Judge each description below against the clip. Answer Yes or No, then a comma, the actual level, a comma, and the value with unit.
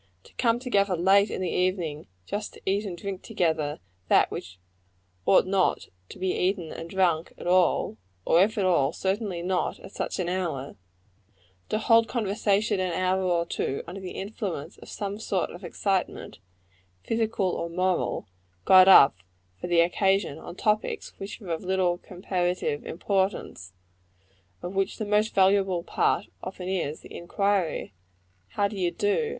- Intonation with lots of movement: No, narrow, 2.5 semitones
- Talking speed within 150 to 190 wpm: Yes, average, 160 wpm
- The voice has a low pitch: No, medium, 185 Hz